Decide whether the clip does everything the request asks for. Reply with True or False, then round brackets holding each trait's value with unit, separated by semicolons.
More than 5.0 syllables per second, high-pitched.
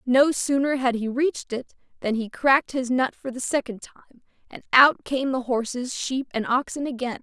True (5.2 syllables/s; 255 Hz)